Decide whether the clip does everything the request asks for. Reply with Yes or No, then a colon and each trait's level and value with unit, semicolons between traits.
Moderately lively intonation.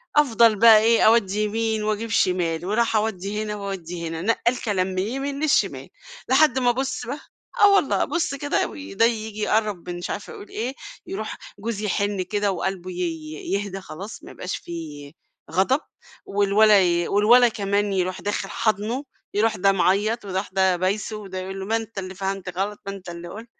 Yes: average, 3.2 semitones